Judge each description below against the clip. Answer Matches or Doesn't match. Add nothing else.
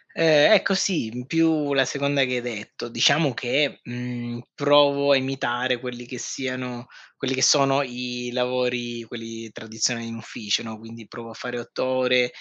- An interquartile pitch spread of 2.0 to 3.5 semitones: Matches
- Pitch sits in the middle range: Doesn't match